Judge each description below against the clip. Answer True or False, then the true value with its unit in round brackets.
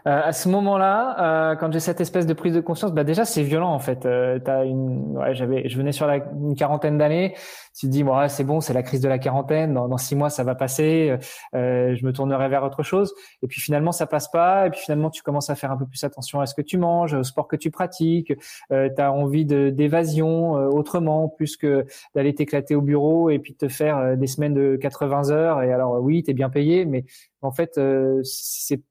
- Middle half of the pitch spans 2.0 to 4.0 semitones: True (2.8 semitones)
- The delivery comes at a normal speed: False (250 wpm)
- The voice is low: False (145 Hz)